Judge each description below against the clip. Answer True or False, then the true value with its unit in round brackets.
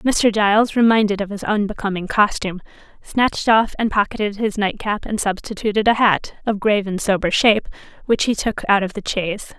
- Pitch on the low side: False (210 Hz)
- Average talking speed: True (180 wpm)